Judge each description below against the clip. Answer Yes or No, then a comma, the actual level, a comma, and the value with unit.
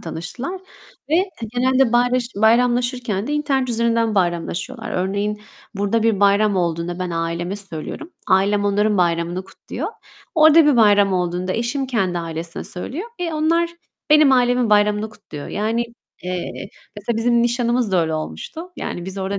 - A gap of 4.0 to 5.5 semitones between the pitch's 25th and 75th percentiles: Yes, average, 5.2 semitones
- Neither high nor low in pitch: No, high, 210 Hz